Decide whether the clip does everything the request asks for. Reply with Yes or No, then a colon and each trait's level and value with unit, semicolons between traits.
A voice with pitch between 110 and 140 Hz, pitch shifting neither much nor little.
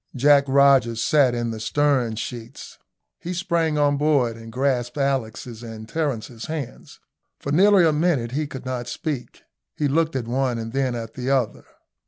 Yes: low, 135 Hz; average, 3.9 semitones